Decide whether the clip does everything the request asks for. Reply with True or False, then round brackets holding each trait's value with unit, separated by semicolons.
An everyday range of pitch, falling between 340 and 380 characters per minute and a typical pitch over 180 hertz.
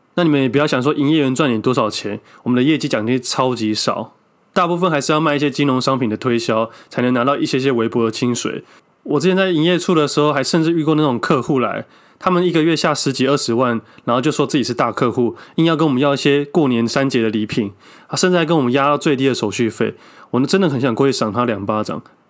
False (4.2 semitones; 370 characters per minute; 135 Hz)